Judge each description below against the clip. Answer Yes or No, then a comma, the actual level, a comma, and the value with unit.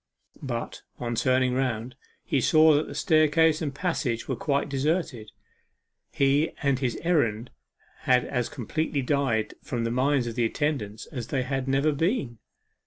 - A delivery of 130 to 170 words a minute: Yes, average, 160 wpm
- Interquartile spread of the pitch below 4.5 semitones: Yes, average, 3.5 semitones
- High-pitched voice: No, low, 135 Hz